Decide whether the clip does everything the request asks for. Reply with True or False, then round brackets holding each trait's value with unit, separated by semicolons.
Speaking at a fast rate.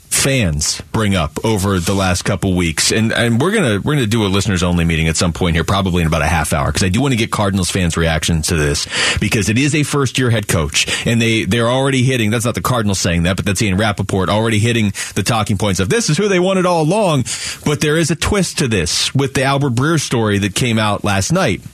True (255 wpm)